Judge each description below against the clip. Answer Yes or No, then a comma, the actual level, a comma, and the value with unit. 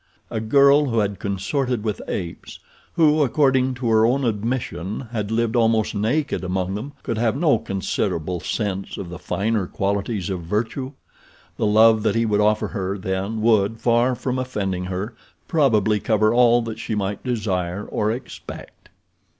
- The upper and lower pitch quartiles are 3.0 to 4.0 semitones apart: Yes, average, 3.4 semitones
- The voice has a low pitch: Yes, low, 110 Hz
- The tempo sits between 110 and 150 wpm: No, average, 160 wpm